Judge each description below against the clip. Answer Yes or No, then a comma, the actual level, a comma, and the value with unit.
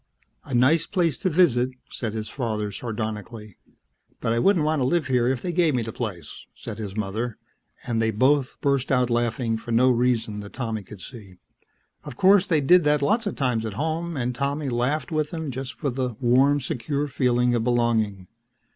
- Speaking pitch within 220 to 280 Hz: No, low, 125 Hz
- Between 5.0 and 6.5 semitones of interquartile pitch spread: No, average, 4.3 semitones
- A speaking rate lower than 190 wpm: No, average, 200 wpm